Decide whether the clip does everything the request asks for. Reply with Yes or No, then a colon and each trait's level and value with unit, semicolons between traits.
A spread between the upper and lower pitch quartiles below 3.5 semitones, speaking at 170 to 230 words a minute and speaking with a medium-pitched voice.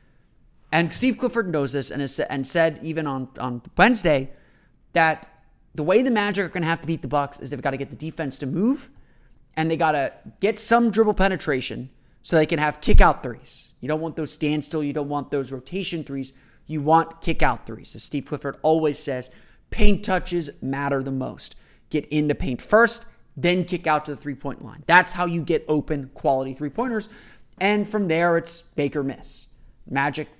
No: average, 4.0 semitones; fast, 205 wpm; medium, 155 Hz